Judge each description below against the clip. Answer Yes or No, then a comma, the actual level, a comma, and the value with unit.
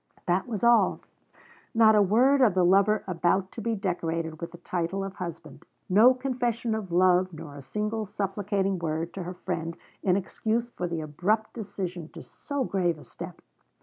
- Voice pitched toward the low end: No, high, 190 Hz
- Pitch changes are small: No, average, 4.0 semitones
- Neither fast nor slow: Yes, average, 180 wpm